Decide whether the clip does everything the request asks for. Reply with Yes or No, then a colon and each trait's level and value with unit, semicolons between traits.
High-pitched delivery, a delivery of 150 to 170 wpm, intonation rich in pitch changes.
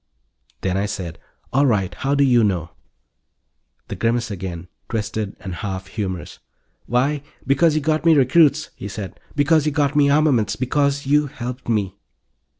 No: low, 125 Hz; average, 155 wpm; wide, 6.4 semitones